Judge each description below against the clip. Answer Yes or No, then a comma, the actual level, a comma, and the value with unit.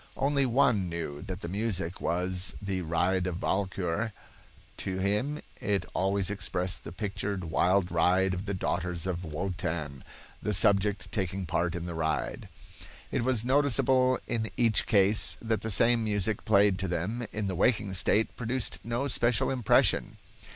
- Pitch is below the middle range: Yes, low, 100 Hz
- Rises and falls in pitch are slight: No, average, 3.7 semitones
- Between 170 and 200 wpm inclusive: No, average, 155 wpm